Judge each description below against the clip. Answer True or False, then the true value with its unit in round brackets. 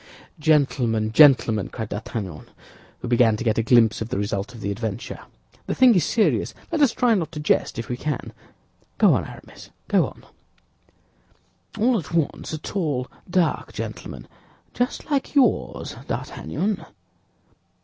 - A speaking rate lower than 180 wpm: True (150 wpm)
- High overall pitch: False (130 Hz)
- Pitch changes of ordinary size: False (8.6 semitones)